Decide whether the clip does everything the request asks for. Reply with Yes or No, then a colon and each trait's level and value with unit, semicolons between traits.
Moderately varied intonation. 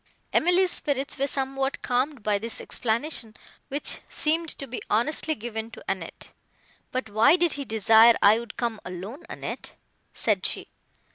Yes: average, 4.5 semitones